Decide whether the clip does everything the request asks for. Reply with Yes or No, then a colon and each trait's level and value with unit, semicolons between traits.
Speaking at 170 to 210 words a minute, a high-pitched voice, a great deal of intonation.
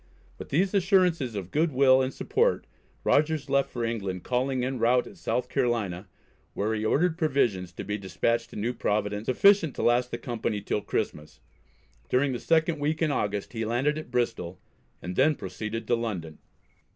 No: average, 175 wpm; low, 125 Hz; wide, 5.8 semitones